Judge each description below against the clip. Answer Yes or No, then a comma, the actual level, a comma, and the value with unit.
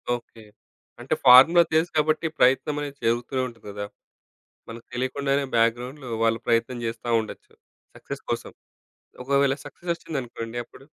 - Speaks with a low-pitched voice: Yes, low, 125 Hz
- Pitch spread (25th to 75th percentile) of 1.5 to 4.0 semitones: Yes, average, 3.5 semitones